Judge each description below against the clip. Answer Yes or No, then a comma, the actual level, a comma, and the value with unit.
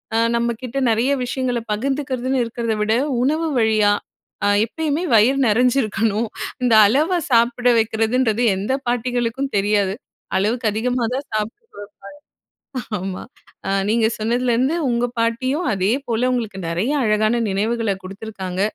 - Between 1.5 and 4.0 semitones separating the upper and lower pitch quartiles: Yes, average, 2.8 semitones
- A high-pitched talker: Yes, high, 230 Hz